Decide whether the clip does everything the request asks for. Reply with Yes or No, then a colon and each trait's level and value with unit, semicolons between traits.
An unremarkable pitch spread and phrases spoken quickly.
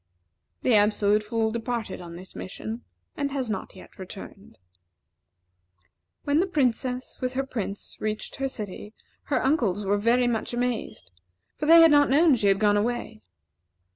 No: average, 4.2 semitones; average, 155 wpm